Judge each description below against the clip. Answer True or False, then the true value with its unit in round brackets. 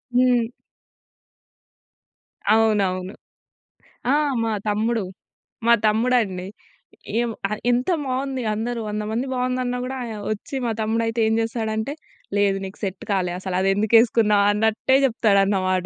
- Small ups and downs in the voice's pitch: False (3.1 semitones)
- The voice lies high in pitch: True (220 Hz)